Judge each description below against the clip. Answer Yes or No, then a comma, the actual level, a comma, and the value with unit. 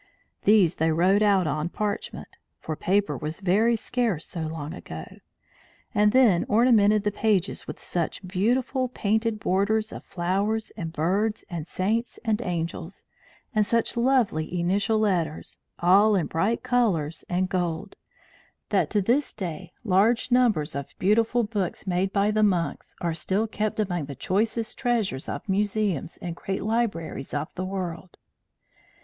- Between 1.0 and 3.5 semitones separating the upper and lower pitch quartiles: No, average, 4.2 semitones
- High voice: Yes, high, 195 Hz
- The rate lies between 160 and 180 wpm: No, average, 150 wpm